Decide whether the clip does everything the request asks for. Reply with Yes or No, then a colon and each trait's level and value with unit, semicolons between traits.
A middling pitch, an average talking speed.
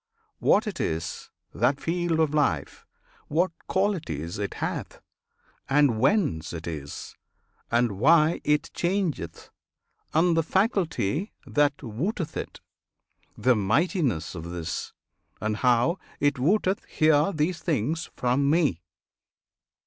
No: medium, 145 Hz; slow, 120 wpm